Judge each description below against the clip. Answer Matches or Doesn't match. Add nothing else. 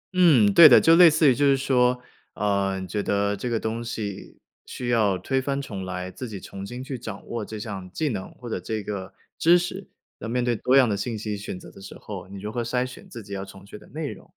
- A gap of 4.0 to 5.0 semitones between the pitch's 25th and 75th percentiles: Matches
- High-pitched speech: Doesn't match